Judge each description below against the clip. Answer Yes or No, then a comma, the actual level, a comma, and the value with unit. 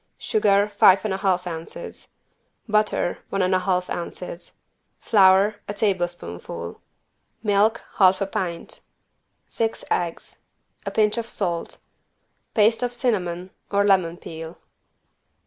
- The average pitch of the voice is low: No, high, 195 Hz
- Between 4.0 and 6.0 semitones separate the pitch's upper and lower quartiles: No, average, 3.2 semitones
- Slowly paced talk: Yes, slow, 120 wpm